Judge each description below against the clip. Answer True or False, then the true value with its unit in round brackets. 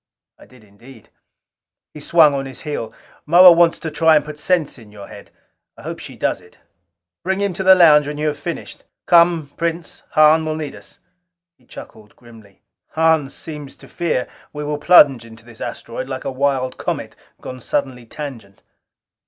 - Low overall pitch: False (150 Hz)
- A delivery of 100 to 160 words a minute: False (180 wpm)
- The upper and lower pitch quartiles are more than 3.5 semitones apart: True (4.3 semitones)